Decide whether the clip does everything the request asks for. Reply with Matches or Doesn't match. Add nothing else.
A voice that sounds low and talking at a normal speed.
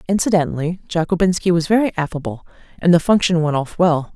Doesn't match